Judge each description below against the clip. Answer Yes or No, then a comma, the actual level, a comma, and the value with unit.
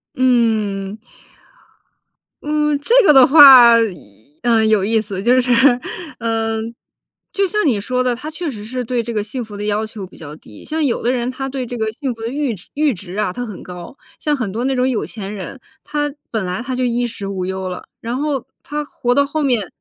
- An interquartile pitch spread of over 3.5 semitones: Yes, average, 4.1 semitones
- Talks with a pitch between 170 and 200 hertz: No, high, 240 Hz